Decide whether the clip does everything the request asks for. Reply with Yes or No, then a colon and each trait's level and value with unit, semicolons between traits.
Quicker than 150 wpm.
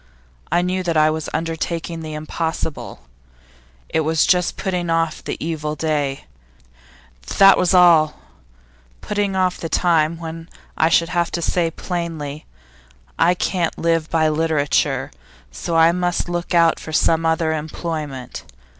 No: average, 140 wpm